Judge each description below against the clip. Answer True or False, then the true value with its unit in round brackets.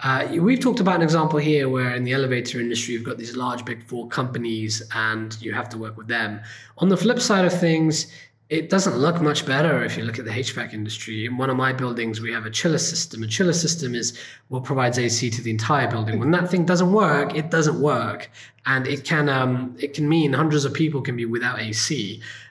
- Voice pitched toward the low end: True (130 Hz)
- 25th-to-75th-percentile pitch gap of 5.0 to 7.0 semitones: True (5.3 semitones)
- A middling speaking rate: False (230 wpm)